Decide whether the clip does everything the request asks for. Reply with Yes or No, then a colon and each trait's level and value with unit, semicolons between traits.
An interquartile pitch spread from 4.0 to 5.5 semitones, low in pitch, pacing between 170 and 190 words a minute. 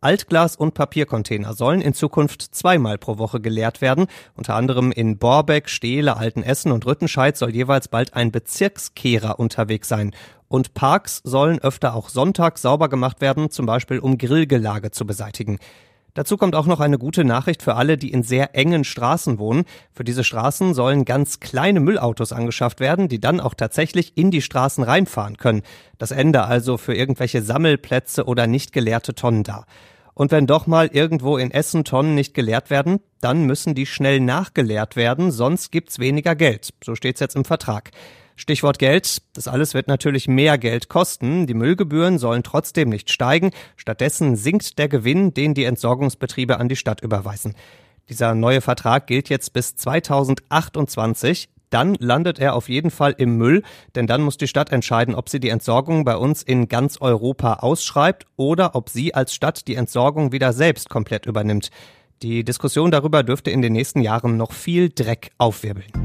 Yes: average, 4.3 semitones; low, 130 Hz; average, 175 wpm